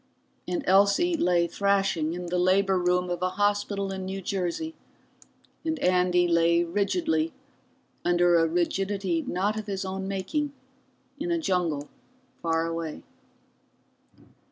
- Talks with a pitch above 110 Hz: Yes, medium, 185 Hz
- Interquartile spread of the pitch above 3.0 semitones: No, narrow, 2.4 semitones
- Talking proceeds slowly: Yes, slow, 130 wpm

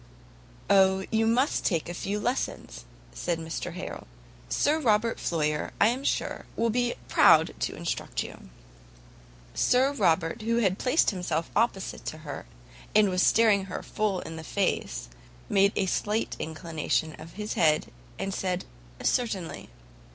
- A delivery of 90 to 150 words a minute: Yes, average, 145 wpm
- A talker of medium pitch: No, high, 195 Hz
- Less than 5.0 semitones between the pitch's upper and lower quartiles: No, average, 5.3 semitones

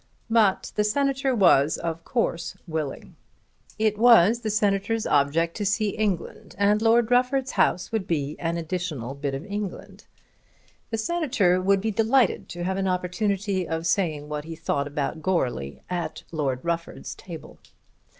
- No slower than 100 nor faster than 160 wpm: Yes, average, 150 wpm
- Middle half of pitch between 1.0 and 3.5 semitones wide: No, average, 4.9 semitones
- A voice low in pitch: No, medium, 185 Hz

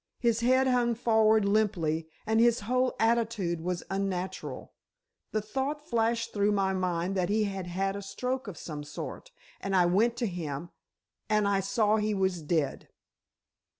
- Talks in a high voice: Yes, high, 205 Hz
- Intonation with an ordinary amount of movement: Yes, average, 4.0 semitones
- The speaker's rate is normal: Yes, average, 155 wpm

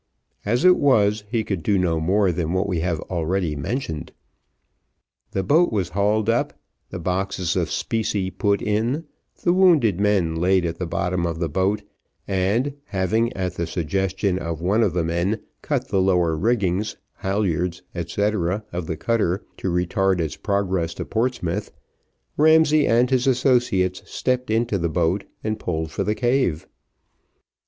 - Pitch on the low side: Yes, very low, 95 Hz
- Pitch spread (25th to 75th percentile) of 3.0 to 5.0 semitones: Yes, average, 4.2 semitones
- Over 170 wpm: No, average, 160 wpm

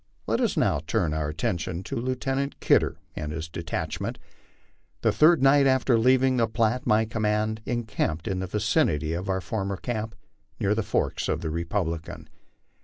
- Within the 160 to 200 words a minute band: Yes, average, 165 wpm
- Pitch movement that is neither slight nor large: No, wide, 6.4 semitones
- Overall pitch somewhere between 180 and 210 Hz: No, low, 105 Hz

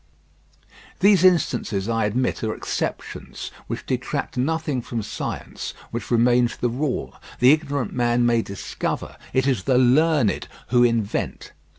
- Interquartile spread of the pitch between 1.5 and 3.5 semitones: Yes, average, 3.2 semitones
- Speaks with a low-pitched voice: Yes, low, 125 Hz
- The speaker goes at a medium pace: No, slow, 130 wpm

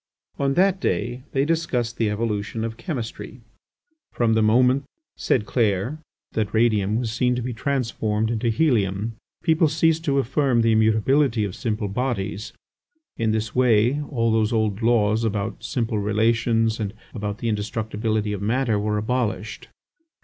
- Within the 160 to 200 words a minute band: No, average, 150 wpm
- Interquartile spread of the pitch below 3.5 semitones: Yes, average, 2.8 semitones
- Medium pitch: No, low, 115 Hz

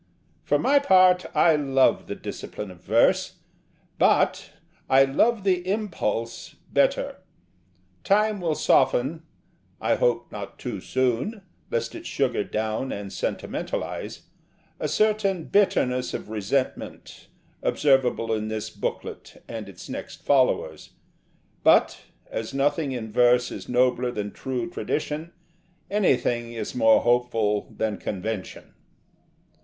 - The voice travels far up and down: Yes, wide, 7.1 semitones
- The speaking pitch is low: Yes, low, 125 Hz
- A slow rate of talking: Yes, slow, 115 wpm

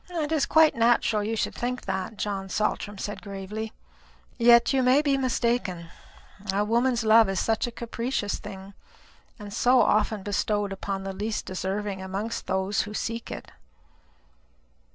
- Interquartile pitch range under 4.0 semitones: Yes, average, 3.3 semitones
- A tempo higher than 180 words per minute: No, average, 155 wpm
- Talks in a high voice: Yes, high, 215 Hz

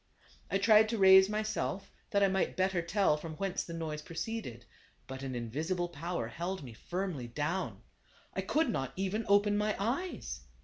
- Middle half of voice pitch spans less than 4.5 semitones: No, average, 5.1 semitones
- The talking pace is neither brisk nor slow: Yes, average, 170 wpm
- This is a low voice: No, medium, 185 Hz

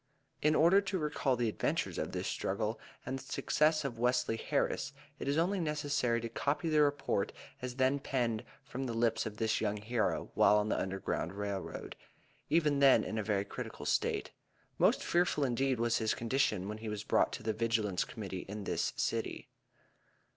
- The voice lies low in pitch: Yes, low, 120 Hz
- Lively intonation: No, average, 4.8 semitones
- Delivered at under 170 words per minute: No, average, 185 wpm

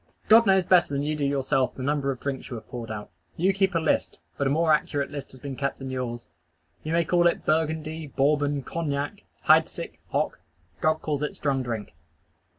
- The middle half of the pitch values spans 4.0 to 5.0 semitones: No, average, 2.9 semitones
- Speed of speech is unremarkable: No, fast, 210 wpm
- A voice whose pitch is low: No, medium, 145 Hz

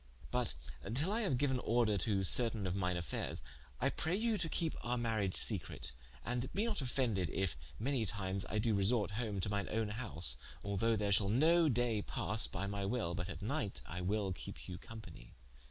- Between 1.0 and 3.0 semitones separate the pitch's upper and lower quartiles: No, average, 4.2 semitones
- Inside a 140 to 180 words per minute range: No, average, 195 wpm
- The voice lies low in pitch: Yes, low, 110 Hz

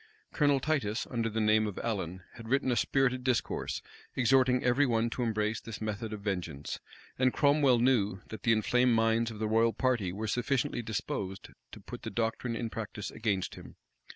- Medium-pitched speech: No, low, 115 Hz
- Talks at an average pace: Yes, average, 180 wpm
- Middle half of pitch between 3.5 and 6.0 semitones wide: No, average, 2.8 semitones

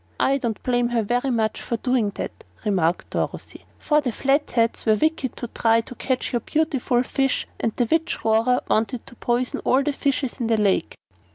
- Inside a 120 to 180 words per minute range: No, average, 190 wpm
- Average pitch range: Yes, average, 3.1 semitones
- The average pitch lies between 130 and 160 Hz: No, high, 245 Hz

